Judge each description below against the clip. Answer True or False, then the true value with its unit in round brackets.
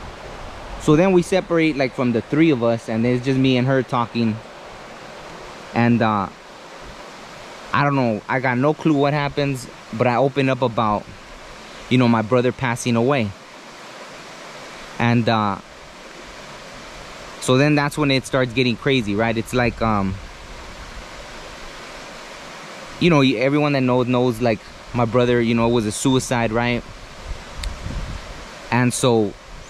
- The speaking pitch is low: True (125 Hz)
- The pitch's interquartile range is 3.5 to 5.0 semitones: False (2.8 semitones)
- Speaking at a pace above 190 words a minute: False (145 wpm)